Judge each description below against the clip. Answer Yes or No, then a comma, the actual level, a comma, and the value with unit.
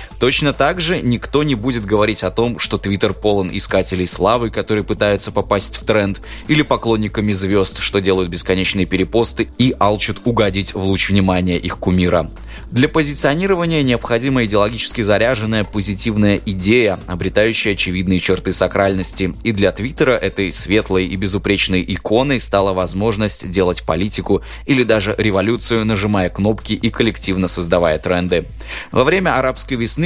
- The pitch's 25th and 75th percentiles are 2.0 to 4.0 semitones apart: Yes, average, 3.3 semitones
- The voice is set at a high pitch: No, low, 100 Hz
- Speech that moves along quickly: No, average, 140 wpm